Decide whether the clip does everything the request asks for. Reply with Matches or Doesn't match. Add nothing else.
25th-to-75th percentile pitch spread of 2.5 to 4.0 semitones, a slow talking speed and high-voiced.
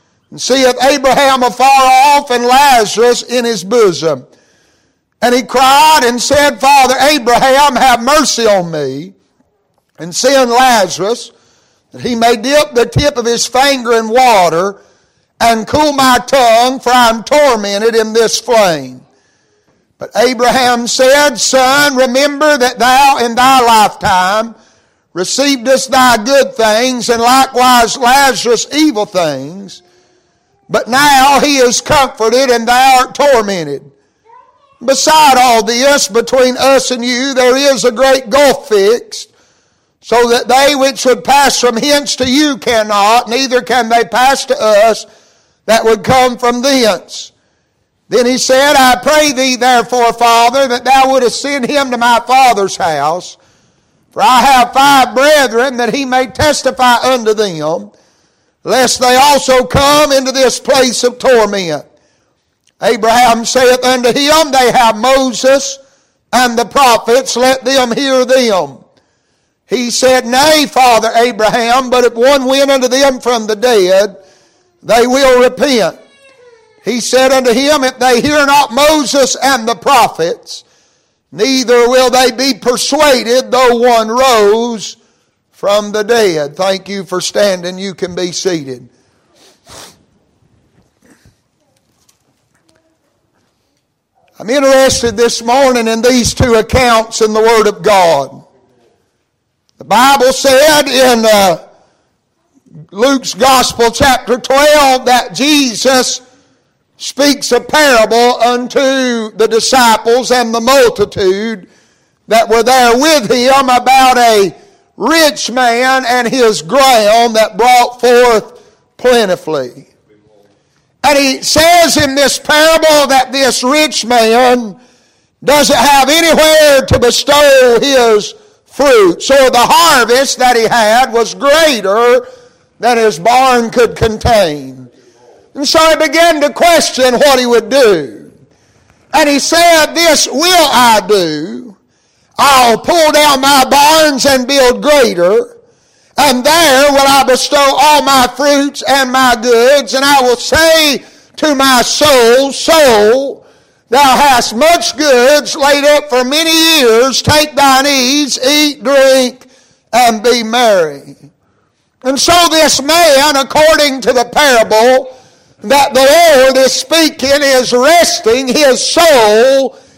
Matches